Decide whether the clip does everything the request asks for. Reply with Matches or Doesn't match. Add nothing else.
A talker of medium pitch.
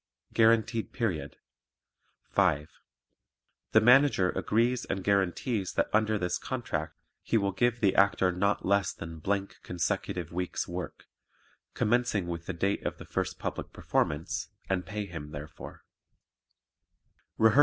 Doesn't match